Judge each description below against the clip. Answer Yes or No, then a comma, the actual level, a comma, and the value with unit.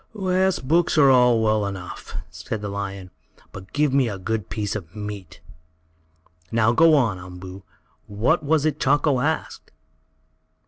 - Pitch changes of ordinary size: No, wide, 6.6 semitones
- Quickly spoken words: No, average, 145 wpm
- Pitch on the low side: Yes, low, 110 Hz